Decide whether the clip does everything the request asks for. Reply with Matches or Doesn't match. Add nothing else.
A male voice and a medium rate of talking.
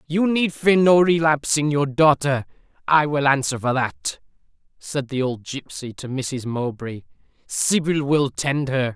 Matches